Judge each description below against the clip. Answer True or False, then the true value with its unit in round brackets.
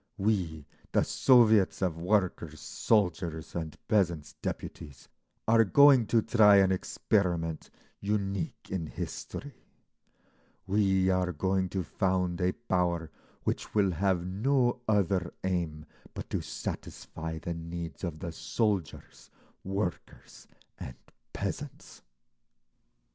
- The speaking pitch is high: False (95 Hz)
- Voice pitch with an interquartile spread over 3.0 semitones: True (3.6 semitones)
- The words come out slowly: True (110 wpm)